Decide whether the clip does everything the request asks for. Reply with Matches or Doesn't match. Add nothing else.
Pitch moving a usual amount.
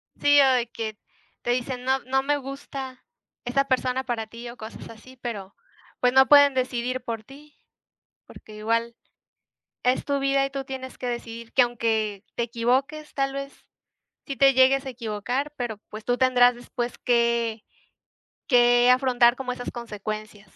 Doesn't match